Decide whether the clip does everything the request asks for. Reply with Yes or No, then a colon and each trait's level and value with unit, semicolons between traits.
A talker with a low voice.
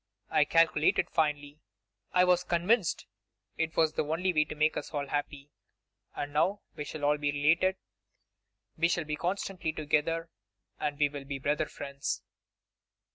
No: medium, 155 Hz